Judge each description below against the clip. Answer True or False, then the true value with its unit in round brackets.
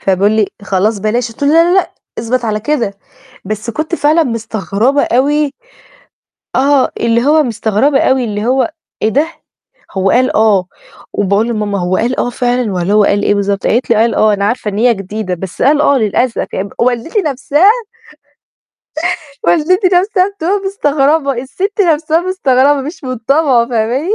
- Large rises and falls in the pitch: True (5.7 semitones)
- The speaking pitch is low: False (245 Hz)